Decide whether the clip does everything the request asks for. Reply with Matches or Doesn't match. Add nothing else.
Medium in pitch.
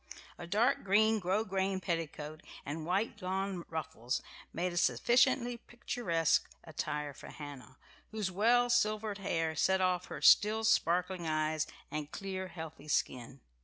Matches